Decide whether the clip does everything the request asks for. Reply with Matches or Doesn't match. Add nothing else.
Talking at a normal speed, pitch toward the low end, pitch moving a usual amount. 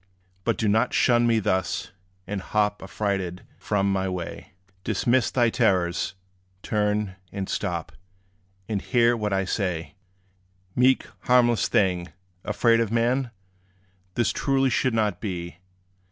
Doesn't match